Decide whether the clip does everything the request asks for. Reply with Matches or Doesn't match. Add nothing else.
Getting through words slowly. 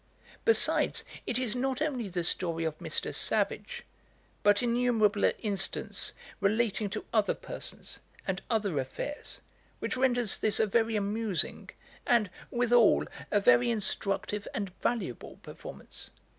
Matches